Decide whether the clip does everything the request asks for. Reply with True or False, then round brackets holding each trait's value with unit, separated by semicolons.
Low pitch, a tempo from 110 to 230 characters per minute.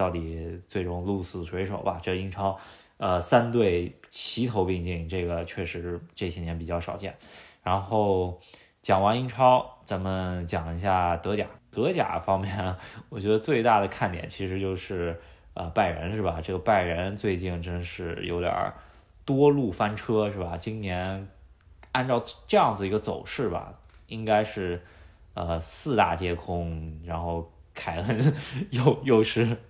True (95 Hz; 215 characters per minute)